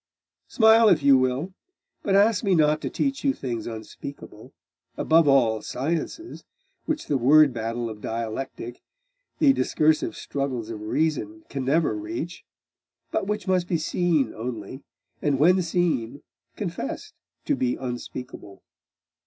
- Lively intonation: Yes, wide, 6.9 semitones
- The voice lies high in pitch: No, medium, 140 Hz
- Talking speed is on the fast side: No, slow, 135 wpm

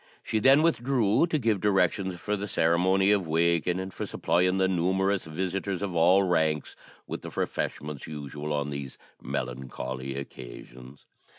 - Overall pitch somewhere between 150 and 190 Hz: No, very low, 90 Hz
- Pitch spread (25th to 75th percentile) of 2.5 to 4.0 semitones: No, average, 4.7 semitones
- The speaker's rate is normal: Yes, average, 150 wpm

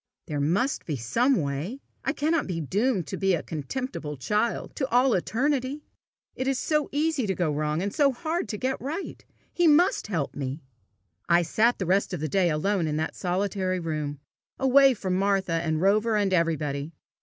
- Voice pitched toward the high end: Yes, high, 195 Hz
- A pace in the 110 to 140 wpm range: No, average, 185 wpm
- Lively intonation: Yes, wide, 8.4 semitones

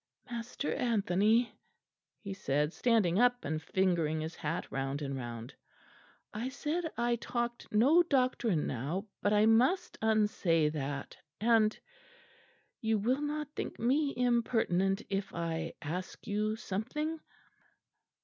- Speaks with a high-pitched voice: Yes, high, 215 Hz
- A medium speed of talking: No, slow, 120 wpm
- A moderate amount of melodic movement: No, wide, 6.5 semitones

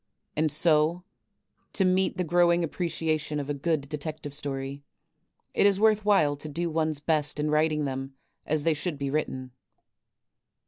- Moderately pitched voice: Yes, medium, 155 Hz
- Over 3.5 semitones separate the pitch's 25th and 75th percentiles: No, average, 2.9 semitones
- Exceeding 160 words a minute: No, average, 155 wpm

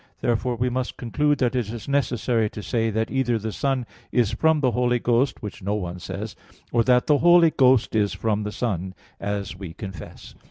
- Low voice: Yes, low, 120 Hz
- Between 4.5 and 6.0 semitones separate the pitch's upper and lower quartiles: No, average, 3.6 semitones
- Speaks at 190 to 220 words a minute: Yes, average, 200 wpm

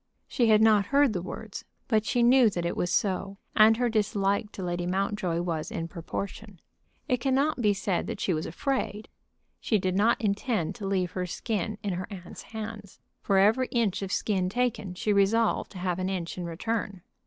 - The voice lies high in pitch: Yes, high, 200 Hz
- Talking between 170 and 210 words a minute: Yes, average, 195 wpm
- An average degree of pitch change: Yes, average, 3.4 semitones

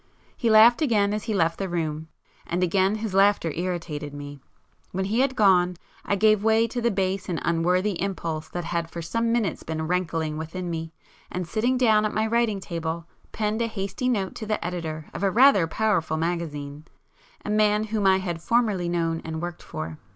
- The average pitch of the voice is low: No, medium, 185 Hz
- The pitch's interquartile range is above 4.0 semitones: Yes, average, 4.5 semitones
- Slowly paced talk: No, average, 195 wpm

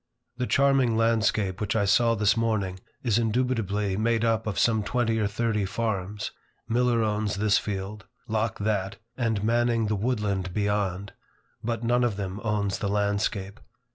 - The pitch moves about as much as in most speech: No, narrow, 2.3 semitones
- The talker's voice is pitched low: Yes, low, 105 Hz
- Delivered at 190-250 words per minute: No, average, 155 wpm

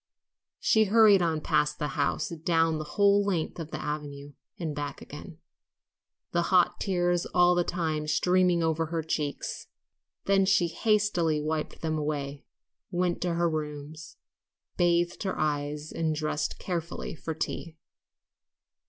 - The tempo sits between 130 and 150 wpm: Yes, average, 140 wpm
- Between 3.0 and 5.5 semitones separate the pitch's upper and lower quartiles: No, narrow, 2.6 semitones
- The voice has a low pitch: No, medium, 165 Hz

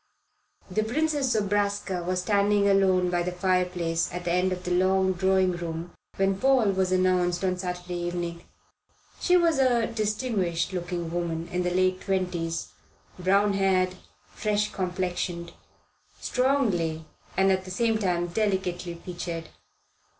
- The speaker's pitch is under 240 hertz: Yes, medium, 185 Hz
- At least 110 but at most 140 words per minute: Yes, slow, 135 wpm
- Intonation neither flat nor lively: No, narrow, 2.3 semitones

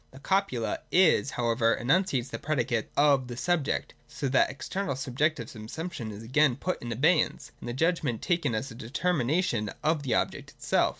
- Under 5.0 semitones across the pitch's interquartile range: No, average, 5.3 semitones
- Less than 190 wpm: Yes, average, 180 wpm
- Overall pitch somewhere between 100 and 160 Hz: Yes, low, 135 Hz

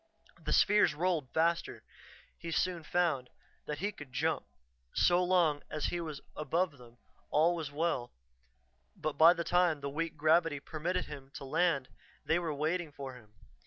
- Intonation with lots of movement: No, average, 3.3 semitones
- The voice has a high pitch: No, medium, 160 Hz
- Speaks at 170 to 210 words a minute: No, average, 160 wpm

